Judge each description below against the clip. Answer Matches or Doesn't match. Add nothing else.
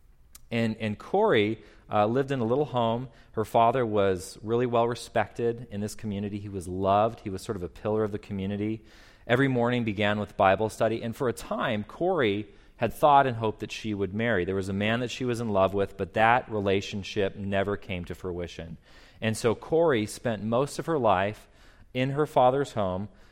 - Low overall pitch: Matches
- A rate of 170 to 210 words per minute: Matches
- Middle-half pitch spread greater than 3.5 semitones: Doesn't match